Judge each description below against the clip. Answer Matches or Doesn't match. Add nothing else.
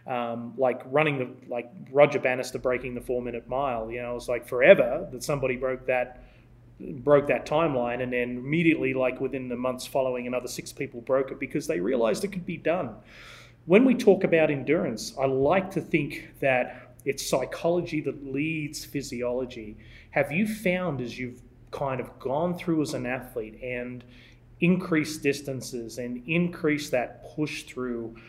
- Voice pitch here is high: Doesn't match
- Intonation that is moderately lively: Matches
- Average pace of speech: Matches